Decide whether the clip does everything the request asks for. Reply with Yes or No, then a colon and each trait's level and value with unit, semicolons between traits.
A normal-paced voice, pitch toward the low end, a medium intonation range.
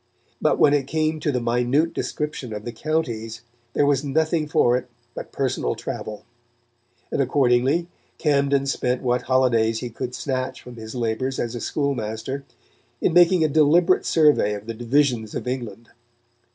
Yes: average, 160 wpm; low, 130 Hz; average, 3.9 semitones